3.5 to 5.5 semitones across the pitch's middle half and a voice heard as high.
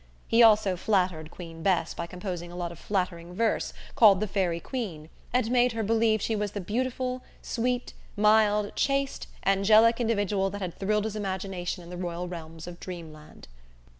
Yes: average, 3.9 semitones; high, 195 Hz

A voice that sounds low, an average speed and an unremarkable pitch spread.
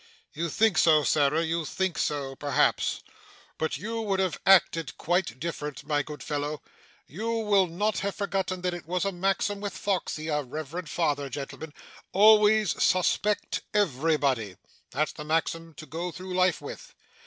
No: medium, 165 Hz; average, 155 wpm; average, 4.4 semitones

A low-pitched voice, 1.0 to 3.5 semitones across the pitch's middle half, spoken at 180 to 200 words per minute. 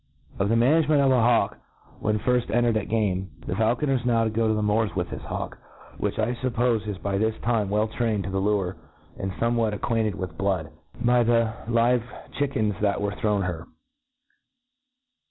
Yes: low, 110 Hz; average, 2.8 semitones; average, 190 wpm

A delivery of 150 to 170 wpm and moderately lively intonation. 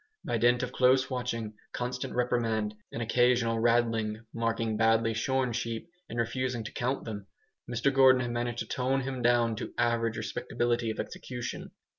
No: average, 160 wpm; narrow, 1.6 semitones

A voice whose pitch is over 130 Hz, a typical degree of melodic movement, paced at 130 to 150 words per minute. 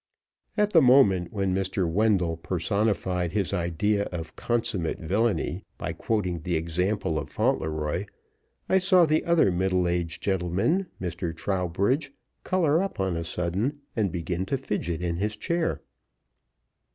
No: very low, 95 Hz; average, 4.6 semitones; average, 140 wpm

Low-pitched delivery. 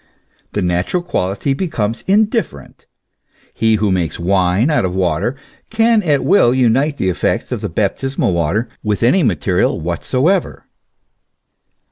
Yes: low, 115 Hz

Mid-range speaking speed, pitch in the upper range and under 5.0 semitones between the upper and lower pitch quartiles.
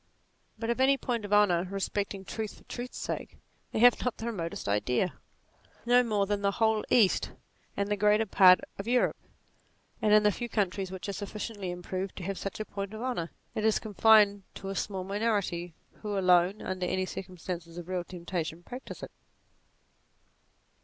Yes: average, 185 wpm; high, 200 Hz; average, 2.9 semitones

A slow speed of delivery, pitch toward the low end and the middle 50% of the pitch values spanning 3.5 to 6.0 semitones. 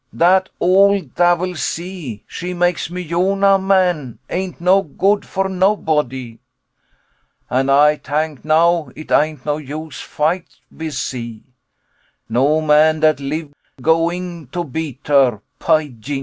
No: slow, 130 wpm; medium, 160 Hz; average, 3.9 semitones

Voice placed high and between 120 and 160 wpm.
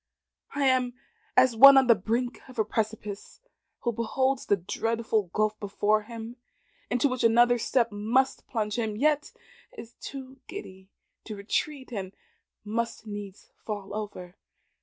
Yes: high, 225 Hz; average, 140 wpm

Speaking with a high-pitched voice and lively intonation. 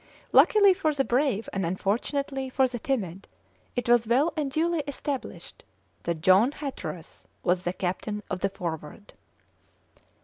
Yes: high, 240 Hz; wide, 6.9 semitones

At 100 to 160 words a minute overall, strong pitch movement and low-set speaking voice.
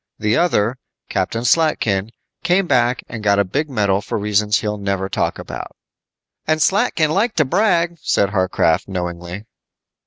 Yes: average, 150 wpm; wide, 8.0 semitones; low, 110 Hz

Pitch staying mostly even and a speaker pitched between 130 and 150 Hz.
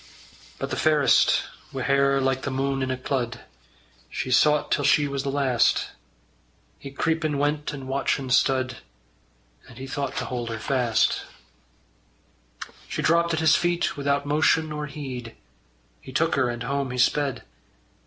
Yes: narrow, 2.3 semitones; medium, 140 Hz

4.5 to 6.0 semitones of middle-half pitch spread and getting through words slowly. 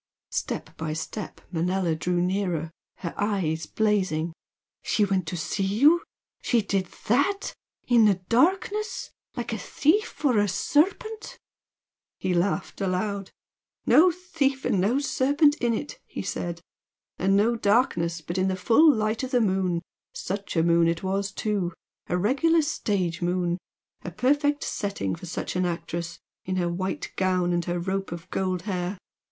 No: wide, 5.5 semitones; average, 155 wpm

